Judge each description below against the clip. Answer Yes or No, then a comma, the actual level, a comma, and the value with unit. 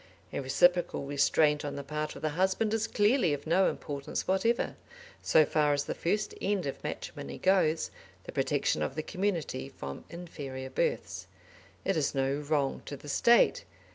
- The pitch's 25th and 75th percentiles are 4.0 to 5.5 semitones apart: Yes, average, 5.1 semitones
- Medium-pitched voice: Yes, medium, 155 Hz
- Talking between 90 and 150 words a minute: No, average, 170 wpm